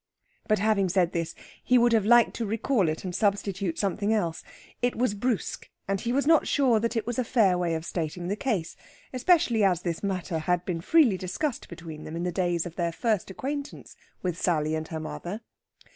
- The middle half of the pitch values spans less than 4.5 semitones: No, average, 5.2 semitones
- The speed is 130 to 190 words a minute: No, fast, 205 wpm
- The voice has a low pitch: No, high, 195 Hz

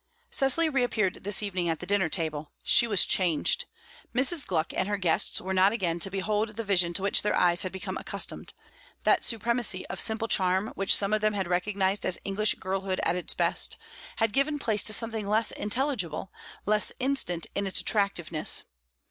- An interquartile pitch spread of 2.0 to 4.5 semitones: Yes, average, 3.2 semitones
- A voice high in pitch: Yes, high, 200 Hz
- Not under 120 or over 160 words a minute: No, average, 185 wpm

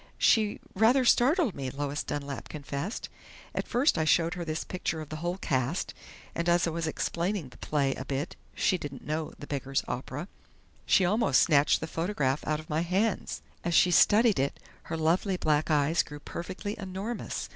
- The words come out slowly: No, average, 180 wpm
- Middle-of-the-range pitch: Yes, medium, 165 Hz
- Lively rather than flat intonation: No, average, 4.5 semitones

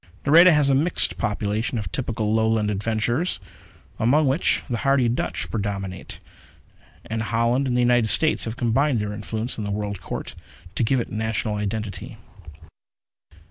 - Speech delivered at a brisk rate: No, average, 150 wpm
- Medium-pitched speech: No, low, 115 Hz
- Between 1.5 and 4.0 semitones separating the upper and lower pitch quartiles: Yes, average, 3.7 semitones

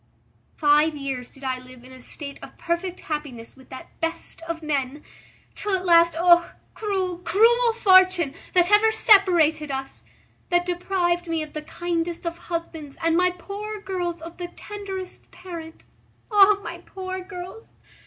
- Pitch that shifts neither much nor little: Yes, average, 3.4 semitones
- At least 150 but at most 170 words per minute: Yes, average, 155 wpm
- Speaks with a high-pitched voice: Yes, very high, 345 Hz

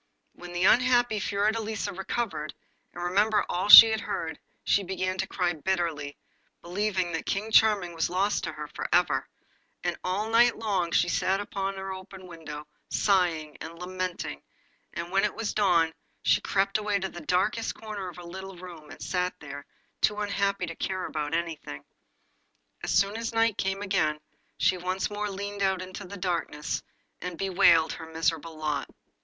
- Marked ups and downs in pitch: No, average, 3.0 semitones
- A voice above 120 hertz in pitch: Yes, medium, 185 Hz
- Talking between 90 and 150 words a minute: No, average, 170 wpm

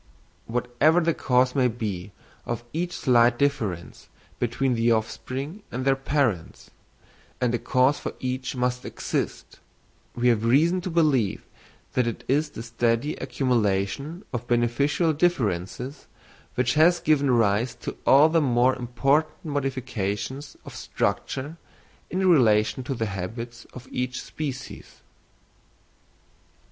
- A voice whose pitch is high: No, low, 125 Hz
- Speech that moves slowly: Yes, slow, 120 wpm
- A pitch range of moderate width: Yes, average, 3.5 semitones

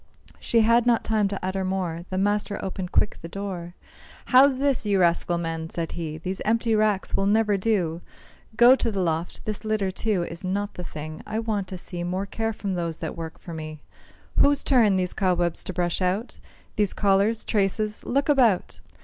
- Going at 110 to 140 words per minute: No, average, 190 wpm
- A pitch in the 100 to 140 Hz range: No, high, 195 Hz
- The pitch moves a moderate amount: Yes, average, 3.8 semitones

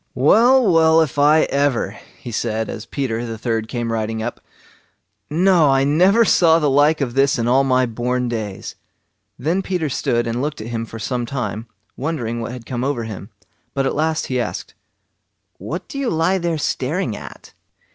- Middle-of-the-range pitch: No, low, 130 Hz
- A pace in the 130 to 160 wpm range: No, average, 185 wpm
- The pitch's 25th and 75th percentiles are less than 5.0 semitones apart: No, average, 5.3 semitones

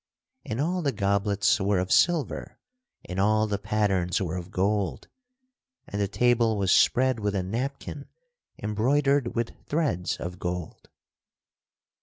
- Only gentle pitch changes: No, average, 4.5 semitones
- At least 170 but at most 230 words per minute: No, slow, 135 wpm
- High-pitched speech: No, low, 105 Hz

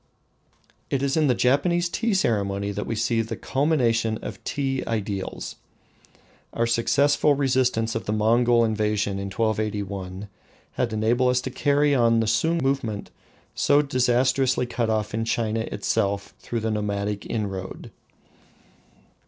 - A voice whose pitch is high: No, low, 115 Hz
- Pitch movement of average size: Yes, average, 3.7 semitones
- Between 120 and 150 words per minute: Yes, slow, 135 wpm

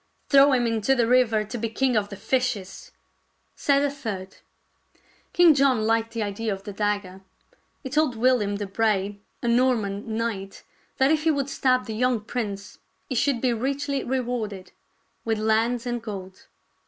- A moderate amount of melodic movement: Yes, average, 3.8 semitones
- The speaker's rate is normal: Yes, average, 170 wpm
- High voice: Yes, high, 230 Hz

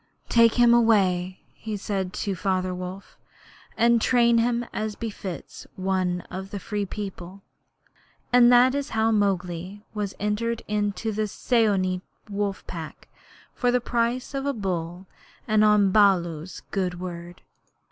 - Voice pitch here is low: No, high, 205 Hz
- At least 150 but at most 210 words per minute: No, slow, 135 wpm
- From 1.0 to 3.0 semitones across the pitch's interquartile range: No, average, 3.7 semitones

